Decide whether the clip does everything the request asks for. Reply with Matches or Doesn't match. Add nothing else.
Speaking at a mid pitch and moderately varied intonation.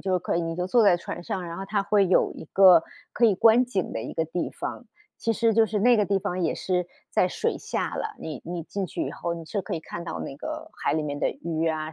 Matches